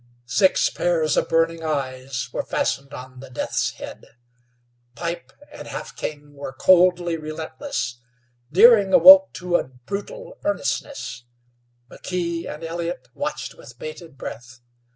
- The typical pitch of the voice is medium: Yes, medium, 165 Hz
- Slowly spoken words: Yes, slow, 125 wpm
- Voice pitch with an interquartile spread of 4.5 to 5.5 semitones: Yes, average, 5.2 semitones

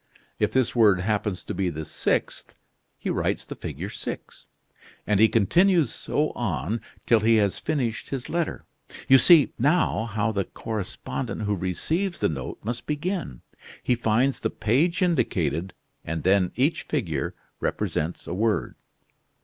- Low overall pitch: Yes, low, 110 Hz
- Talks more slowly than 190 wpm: Yes, average, 150 wpm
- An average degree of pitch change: No, wide, 7.2 semitones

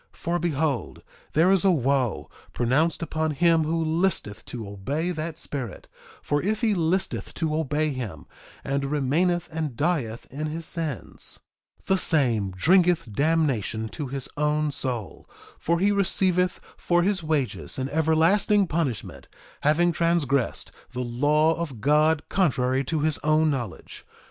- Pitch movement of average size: Yes, average, 4.1 semitones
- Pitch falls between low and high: Yes, medium, 155 Hz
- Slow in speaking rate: No, average, 145 wpm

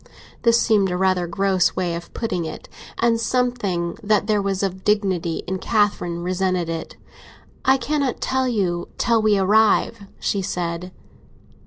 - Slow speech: No, average, 150 wpm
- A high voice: Yes, high, 195 Hz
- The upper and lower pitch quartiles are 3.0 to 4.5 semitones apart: Yes, average, 3.6 semitones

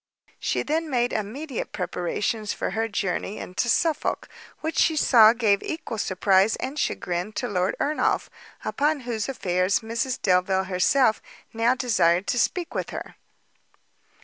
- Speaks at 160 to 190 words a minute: No, average, 140 wpm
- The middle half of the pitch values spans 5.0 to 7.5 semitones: Yes, wide, 5.4 semitones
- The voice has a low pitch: No, high, 225 Hz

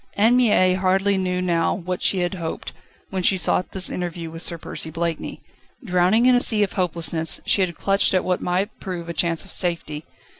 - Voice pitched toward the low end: No, medium, 180 Hz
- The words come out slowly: No, average, 200 wpm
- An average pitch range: No, narrow, 2.2 semitones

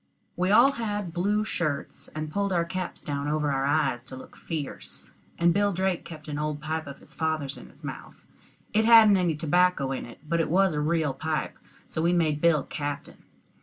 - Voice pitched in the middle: Yes, medium, 160 Hz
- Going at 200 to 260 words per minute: Yes, fast, 205 wpm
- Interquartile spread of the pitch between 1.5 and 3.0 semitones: No, average, 3.6 semitones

